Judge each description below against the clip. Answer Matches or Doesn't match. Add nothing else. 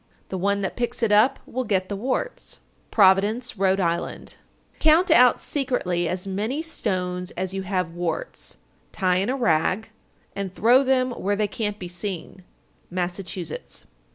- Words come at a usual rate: Matches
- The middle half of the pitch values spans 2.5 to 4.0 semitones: Doesn't match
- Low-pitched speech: Doesn't match